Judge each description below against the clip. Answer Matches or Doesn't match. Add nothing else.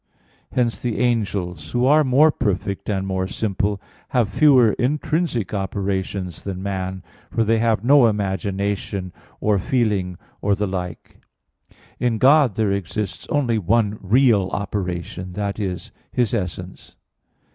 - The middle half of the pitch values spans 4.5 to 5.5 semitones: Doesn't match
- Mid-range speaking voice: Doesn't match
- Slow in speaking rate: Matches